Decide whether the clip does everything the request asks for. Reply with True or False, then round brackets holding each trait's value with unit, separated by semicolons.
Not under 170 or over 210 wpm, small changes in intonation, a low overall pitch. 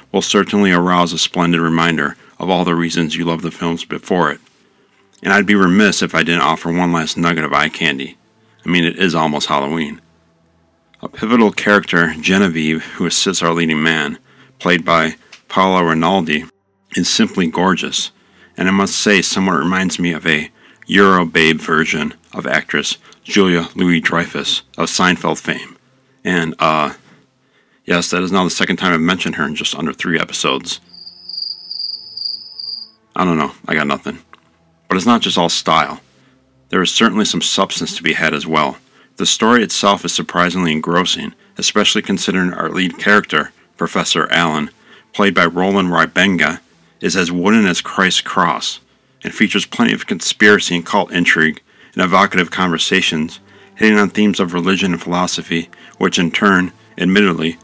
False (160 wpm; 2.3 semitones; 85 Hz)